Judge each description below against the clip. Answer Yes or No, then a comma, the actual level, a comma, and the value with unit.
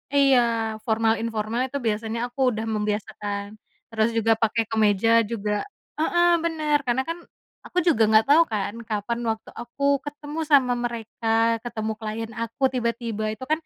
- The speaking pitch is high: Yes, high, 230 Hz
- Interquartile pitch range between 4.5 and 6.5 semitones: No, average, 3.1 semitones